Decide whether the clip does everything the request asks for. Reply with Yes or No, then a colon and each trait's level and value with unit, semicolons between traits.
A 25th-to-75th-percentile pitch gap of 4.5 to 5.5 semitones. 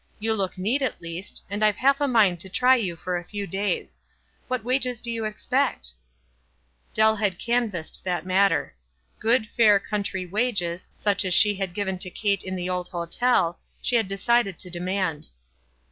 No: average, 3.7 semitones